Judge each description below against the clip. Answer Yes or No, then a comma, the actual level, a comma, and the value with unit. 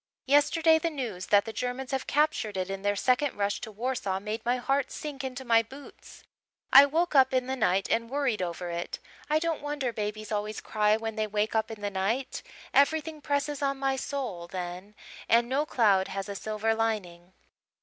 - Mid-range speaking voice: No, high, 230 Hz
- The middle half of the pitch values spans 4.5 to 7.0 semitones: Yes, average, 5.0 semitones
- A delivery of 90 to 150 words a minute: No, average, 195 wpm